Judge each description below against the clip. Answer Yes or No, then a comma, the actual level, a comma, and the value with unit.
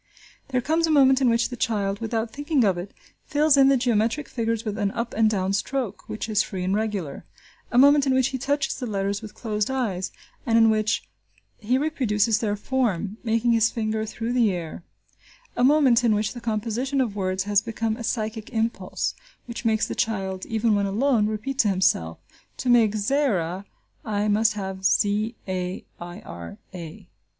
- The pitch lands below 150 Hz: No, high, 220 Hz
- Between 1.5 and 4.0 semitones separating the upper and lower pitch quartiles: Yes, average, 3.4 semitones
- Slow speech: No, average, 190 wpm